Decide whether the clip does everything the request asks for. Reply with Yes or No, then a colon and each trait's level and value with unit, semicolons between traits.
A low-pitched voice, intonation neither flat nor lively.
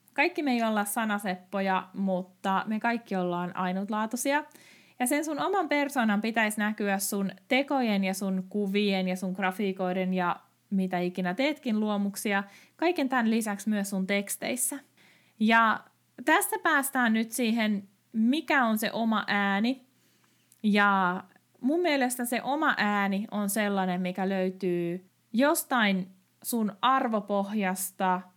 No: high, 210 Hz; average, 4.5 semitones